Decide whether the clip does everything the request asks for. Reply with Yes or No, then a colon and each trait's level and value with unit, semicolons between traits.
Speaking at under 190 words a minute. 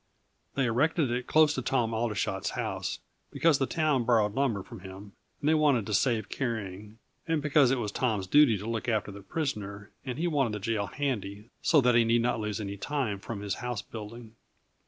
No: average, 200 wpm